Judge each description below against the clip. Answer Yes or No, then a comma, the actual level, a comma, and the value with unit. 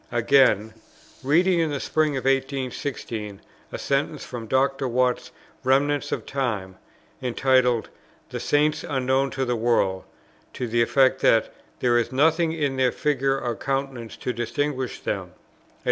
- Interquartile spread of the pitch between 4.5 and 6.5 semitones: No, average, 2.7 semitones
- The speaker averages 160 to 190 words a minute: No, average, 145 wpm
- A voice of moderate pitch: No, low, 130 Hz